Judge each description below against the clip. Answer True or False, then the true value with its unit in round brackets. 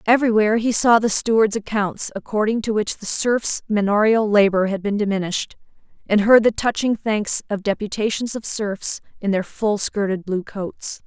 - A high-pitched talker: True (210 Hz)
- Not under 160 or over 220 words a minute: True (170 wpm)